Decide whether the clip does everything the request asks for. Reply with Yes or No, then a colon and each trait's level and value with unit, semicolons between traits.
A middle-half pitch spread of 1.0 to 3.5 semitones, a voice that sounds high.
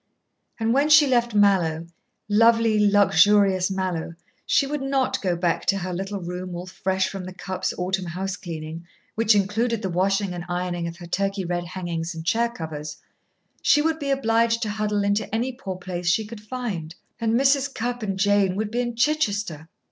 No: average, 4.3 semitones; high, 200 Hz